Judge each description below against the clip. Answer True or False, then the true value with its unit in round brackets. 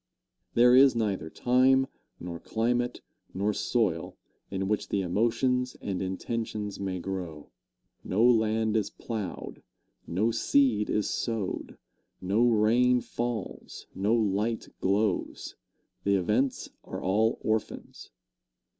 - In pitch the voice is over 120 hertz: False (110 Hz)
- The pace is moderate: False (110 wpm)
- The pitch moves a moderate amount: True (3.5 semitones)